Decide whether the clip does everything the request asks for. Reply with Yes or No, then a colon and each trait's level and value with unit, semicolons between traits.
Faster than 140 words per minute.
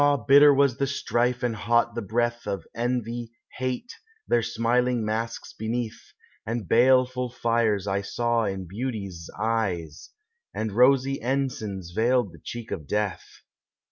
No: slow, 135 wpm